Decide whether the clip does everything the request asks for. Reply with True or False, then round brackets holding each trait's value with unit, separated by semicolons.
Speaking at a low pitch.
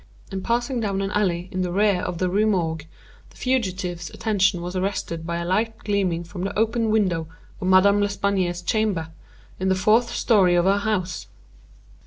False (190 Hz)